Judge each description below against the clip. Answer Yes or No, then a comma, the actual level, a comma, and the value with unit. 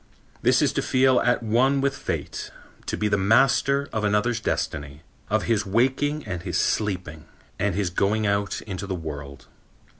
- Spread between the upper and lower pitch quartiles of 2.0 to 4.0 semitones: No, average, 5.0 semitones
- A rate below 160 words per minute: No, average, 170 wpm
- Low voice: Yes, low, 105 Hz